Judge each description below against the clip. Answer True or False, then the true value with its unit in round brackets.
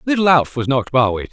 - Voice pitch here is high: False (140 Hz)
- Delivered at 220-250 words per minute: True (225 wpm)